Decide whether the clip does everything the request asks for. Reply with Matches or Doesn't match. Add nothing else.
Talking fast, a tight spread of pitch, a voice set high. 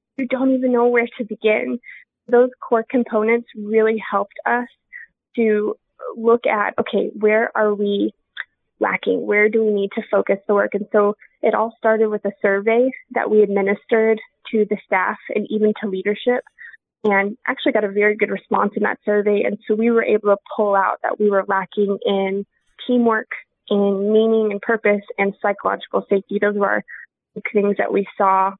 Doesn't match